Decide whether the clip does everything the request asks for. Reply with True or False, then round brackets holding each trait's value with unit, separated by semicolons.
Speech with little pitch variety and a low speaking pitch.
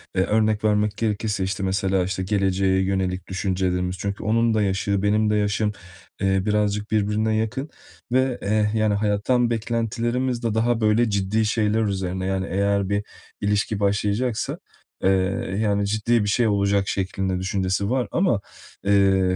True (2.2 semitones; 105 Hz)